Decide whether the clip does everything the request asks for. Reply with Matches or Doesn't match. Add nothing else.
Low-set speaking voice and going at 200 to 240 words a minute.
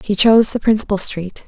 Doesn't match